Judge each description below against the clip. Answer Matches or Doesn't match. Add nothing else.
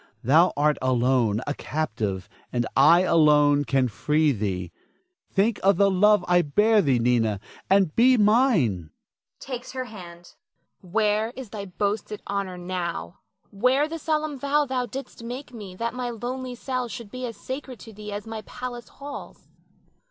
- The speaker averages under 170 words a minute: Matches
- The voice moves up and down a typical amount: Doesn't match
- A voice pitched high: Matches